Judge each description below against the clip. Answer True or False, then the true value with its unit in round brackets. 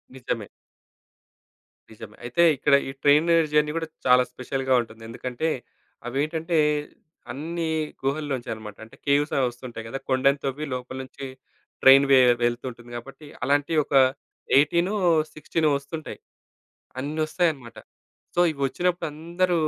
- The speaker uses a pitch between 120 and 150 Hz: True (140 Hz)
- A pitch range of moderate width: True (3.6 semitones)